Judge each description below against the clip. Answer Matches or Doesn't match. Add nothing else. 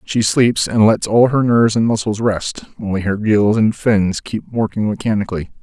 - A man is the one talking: Matches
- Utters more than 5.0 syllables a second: Doesn't match